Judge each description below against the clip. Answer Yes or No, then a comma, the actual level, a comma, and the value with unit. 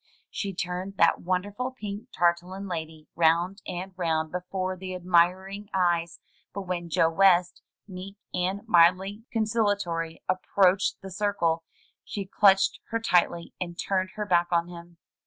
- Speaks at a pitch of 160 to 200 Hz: Yes, medium, 185 Hz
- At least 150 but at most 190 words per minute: No, average, 140 wpm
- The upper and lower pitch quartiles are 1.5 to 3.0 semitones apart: Yes, narrow, 2.4 semitones